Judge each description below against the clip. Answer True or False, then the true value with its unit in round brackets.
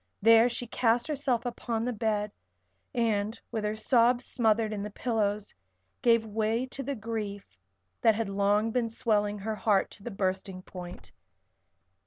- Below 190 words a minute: True (155 wpm)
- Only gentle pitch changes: True (2.3 semitones)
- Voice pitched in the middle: False (220 Hz)